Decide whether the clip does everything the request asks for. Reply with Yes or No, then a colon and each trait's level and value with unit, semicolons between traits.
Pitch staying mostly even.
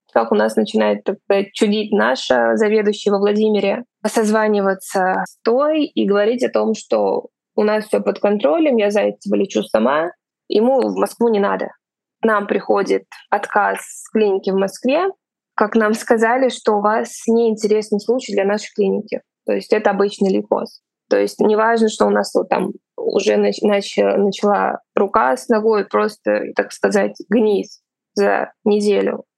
Yes: narrow, 2.1 semitones